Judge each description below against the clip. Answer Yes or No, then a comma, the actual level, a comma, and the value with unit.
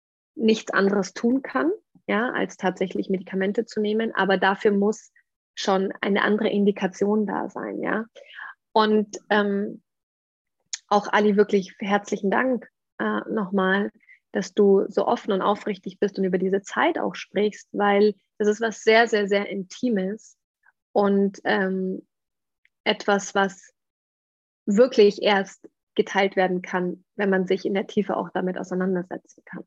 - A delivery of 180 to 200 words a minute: No, average, 140 wpm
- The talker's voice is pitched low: No, high, 205 Hz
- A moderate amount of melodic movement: No, narrow, 1.6 semitones